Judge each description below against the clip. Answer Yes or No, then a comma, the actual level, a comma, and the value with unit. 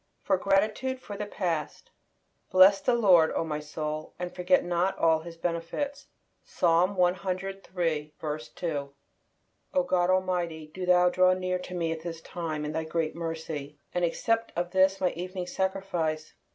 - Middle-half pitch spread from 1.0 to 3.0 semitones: Yes, narrow, 2.6 semitones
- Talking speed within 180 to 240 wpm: No, average, 155 wpm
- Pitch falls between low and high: Yes, medium, 180 Hz